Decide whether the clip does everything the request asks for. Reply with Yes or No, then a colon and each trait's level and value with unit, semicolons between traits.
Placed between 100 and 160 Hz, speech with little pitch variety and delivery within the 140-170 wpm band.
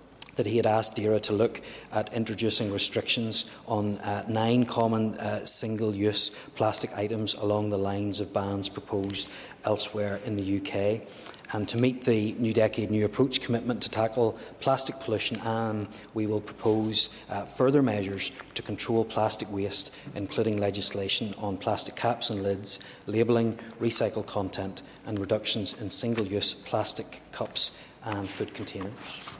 Yes: low, 110 Hz; narrow, 1.9 semitones; average, 145 wpm